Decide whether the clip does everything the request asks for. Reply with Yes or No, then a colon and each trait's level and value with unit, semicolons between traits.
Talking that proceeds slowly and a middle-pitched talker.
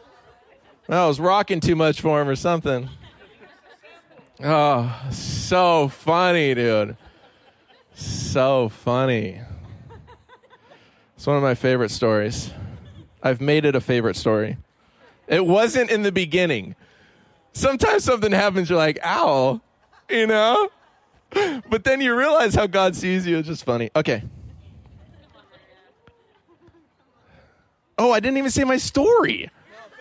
Yes: slow, 120 wpm; medium, 150 Hz